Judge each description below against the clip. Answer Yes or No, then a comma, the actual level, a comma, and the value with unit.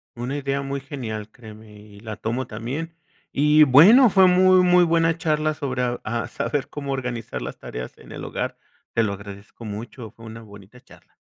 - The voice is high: No, low, 125 Hz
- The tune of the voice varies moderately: No, wide, 5.7 semitones